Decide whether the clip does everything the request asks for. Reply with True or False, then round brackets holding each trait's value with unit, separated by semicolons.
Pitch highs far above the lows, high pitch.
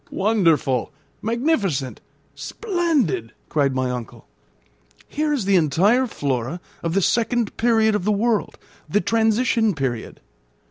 True (8.4 semitones; 205 Hz)